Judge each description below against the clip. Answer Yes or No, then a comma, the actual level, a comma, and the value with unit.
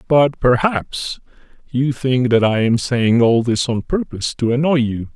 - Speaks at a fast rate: No, average, 175 wpm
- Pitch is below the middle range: Yes, low, 125 Hz